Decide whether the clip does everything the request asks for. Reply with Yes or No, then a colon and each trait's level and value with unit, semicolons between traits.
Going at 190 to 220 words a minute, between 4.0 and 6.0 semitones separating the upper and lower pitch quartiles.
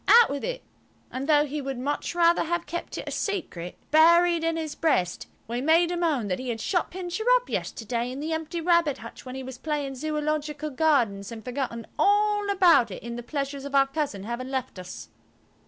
Yes: fast, 205 wpm; average, 4.9 semitones